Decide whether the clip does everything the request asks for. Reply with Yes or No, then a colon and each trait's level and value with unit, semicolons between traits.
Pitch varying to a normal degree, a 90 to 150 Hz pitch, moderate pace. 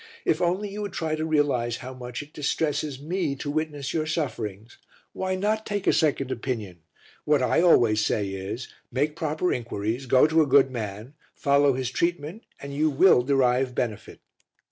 Yes: average, 4.2 semitones; medium, 140 Hz; average, 175 wpm